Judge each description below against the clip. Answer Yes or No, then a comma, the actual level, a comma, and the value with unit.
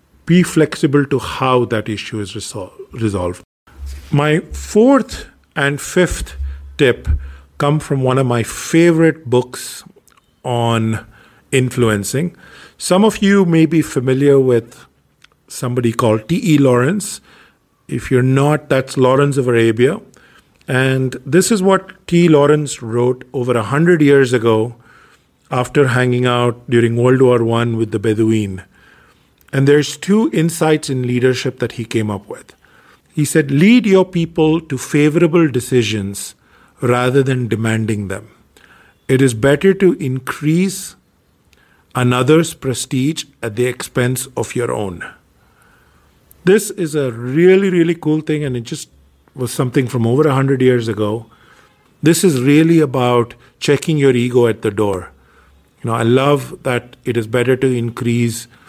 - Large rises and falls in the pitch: No, average, 4.7 semitones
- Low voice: Yes, low, 130 Hz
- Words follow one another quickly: No, average, 140 wpm